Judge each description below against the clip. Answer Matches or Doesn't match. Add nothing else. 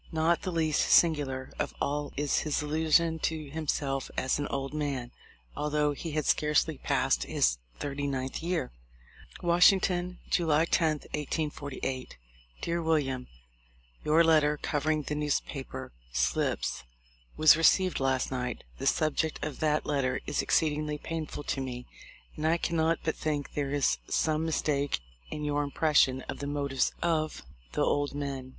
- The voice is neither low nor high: Matches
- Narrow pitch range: Matches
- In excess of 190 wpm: Doesn't match